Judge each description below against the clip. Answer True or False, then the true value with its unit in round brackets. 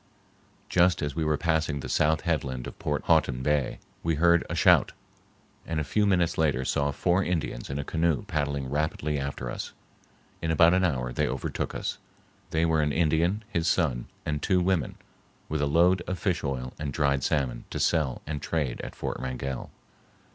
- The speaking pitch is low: True (75 Hz)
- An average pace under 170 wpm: False (185 wpm)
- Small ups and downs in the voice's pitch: False (3.2 semitones)